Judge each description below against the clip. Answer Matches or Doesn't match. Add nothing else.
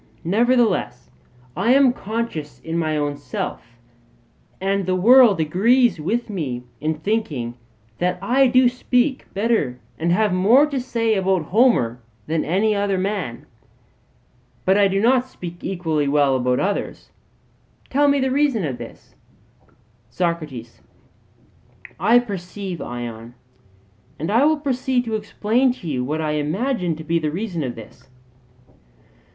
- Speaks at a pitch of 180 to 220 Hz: Matches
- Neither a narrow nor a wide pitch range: Doesn't match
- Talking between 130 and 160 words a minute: Matches